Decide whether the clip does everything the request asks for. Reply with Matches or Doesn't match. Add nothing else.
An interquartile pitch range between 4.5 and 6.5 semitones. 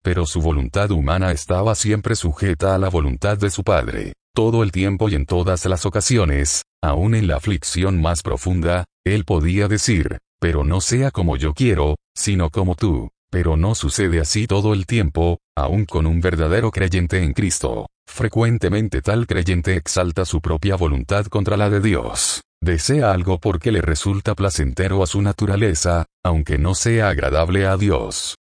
Doesn't match